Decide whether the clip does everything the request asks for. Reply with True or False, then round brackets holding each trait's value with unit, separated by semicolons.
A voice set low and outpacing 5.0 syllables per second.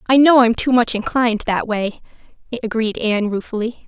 False (235 Hz; 5.6 syllables/s)